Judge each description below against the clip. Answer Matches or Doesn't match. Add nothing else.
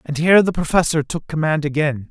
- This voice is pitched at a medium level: Matches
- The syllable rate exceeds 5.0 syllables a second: Matches